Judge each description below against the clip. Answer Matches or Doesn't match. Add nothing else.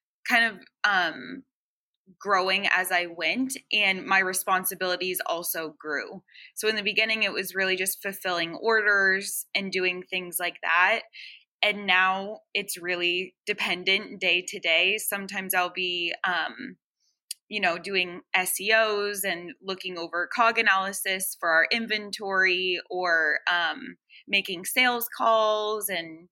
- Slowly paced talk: Matches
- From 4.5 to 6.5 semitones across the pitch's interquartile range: Doesn't match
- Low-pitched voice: Doesn't match